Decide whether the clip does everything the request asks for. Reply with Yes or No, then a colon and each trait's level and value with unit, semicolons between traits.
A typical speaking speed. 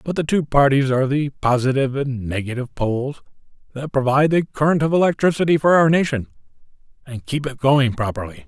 Yes: average, 170 wpm